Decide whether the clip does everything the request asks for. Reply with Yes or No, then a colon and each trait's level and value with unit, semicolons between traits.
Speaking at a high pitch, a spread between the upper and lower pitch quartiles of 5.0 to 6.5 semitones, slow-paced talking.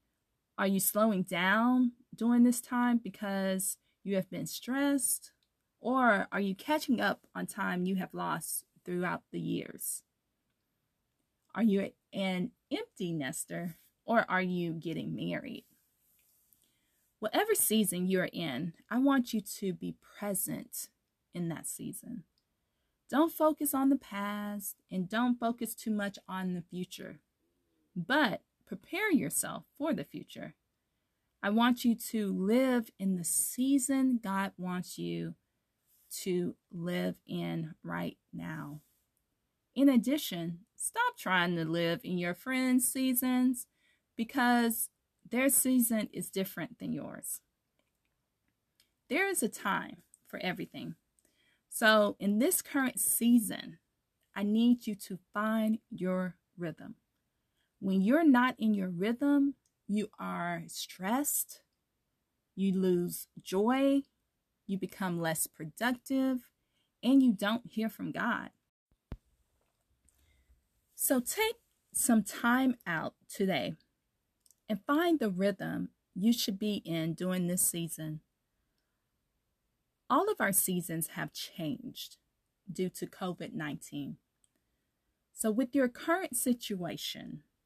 Yes: high, 210 Hz; wide, 5.4 semitones; slow, 120 wpm